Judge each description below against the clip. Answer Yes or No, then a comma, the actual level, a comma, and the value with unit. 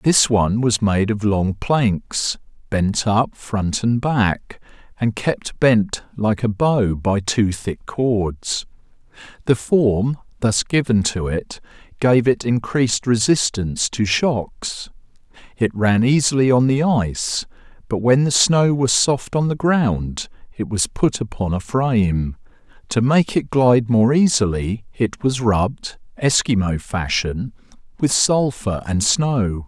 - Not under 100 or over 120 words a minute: No, average, 140 wpm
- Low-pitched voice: Yes, low, 115 Hz